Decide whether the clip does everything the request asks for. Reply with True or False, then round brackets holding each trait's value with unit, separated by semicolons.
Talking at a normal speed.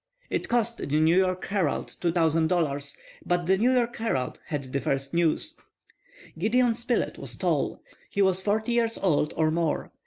True (160 wpm)